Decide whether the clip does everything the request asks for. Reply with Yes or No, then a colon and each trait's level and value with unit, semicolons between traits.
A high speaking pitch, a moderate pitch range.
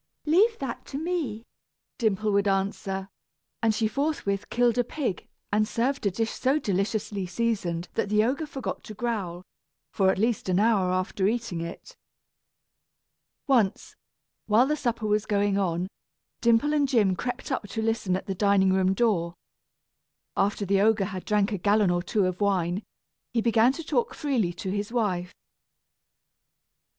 Yes: high, 210 Hz; average, 3.7 semitones